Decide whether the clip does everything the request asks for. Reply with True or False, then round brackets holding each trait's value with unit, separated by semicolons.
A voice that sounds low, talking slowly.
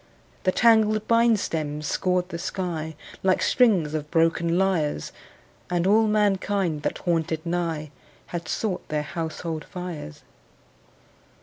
False (175 Hz; 120 wpm)